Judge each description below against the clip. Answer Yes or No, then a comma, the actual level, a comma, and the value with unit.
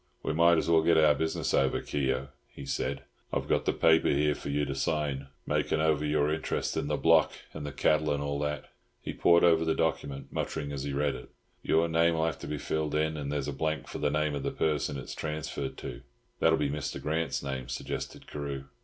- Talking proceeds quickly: Yes, fast, 225 wpm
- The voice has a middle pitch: No, very low, 75 Hz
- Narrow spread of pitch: Yes, narrow, 2.0 semitones